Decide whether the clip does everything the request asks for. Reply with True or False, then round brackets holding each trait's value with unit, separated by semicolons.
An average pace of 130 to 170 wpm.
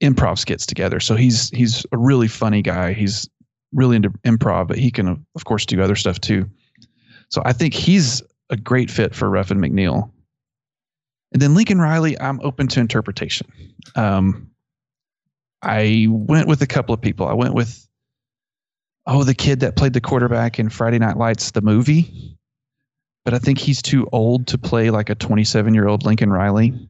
False (180 wpm)